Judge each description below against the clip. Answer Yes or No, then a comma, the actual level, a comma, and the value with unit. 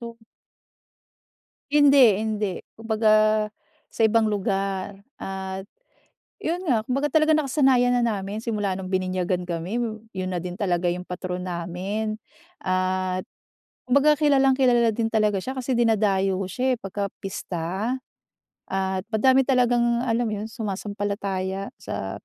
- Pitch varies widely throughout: No, average, 4.2 semitones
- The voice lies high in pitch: Yes, high, 210 Hz